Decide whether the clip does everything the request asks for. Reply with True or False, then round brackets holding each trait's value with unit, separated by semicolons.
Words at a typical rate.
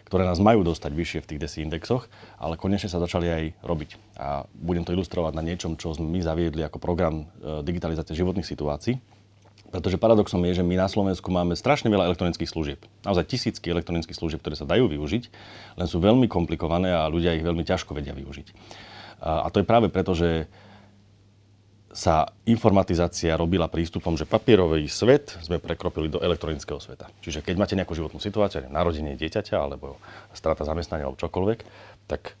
False (170 wpm)